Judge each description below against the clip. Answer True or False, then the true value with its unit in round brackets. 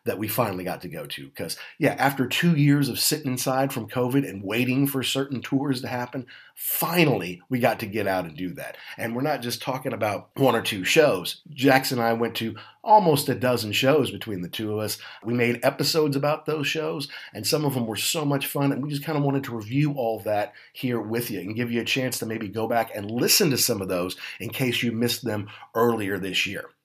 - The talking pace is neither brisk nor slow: False (240 wpm)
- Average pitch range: True (3.9 semitones)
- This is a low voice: True (125 Hz)